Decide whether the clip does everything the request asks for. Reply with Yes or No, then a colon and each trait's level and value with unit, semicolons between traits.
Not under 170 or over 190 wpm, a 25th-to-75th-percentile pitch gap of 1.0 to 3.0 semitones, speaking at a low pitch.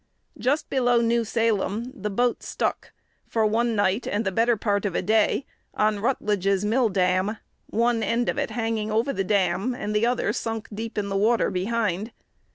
No: average, 180 wpm; narrow, 2.5 semitones; high, 220 Hz